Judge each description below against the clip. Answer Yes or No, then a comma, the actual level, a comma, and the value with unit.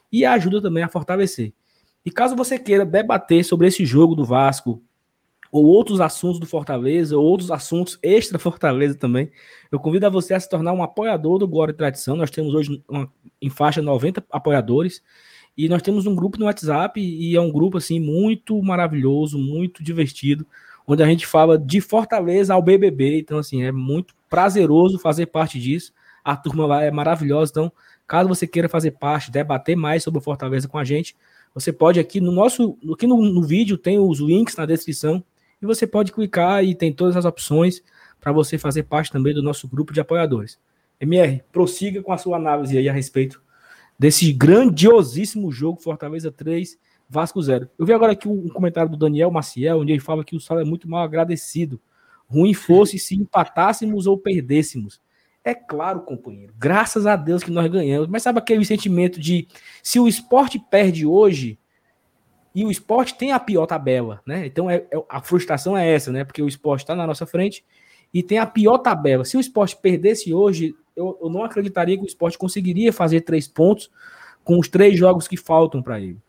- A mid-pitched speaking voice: Yes, medium, 165 Hz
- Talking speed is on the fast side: Yes, fast, 190 wpm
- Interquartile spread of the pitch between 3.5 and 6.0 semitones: Yes, average, 4.3 semitones